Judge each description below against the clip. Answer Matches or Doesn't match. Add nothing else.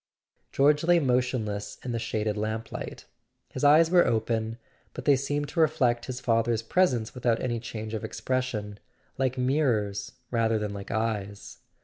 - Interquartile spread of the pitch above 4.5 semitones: Doesn't match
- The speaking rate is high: Doesn't match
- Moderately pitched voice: Doesn't match